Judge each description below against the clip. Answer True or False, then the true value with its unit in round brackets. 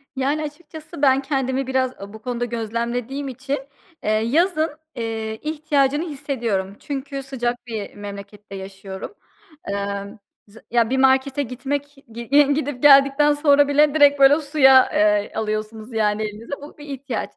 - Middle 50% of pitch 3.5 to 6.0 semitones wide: True (4.5 semitones)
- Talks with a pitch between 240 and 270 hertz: True (265 Hz)